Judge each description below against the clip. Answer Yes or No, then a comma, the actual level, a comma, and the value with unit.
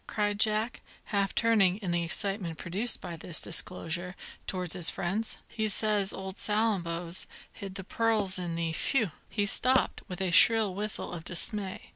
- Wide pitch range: No, average, 3.3 semitones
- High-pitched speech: Yes, high, 195 Hz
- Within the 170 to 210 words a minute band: No, average, 160 wpm